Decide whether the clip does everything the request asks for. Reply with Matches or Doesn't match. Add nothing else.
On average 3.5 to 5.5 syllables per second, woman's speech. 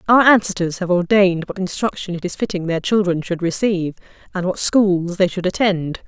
Matches